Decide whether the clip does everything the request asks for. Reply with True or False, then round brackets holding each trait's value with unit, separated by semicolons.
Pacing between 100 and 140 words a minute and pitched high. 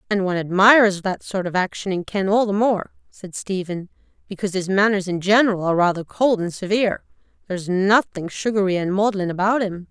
False (190 wpm; 195 Hz)